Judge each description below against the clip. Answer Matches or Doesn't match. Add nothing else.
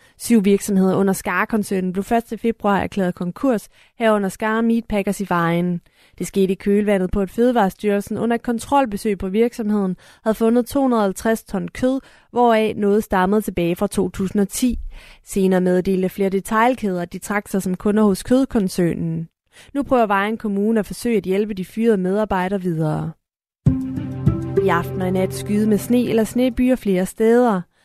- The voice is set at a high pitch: Matches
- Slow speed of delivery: Doesn't match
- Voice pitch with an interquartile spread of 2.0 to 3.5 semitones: Matches